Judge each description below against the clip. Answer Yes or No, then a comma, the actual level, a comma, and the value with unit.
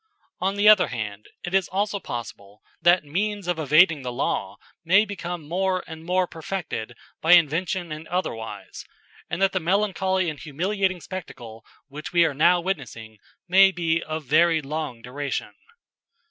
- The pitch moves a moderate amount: Yes, average, 4.7 semitones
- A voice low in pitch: No, medium, 170 Hz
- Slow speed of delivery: No, average, 155 wpm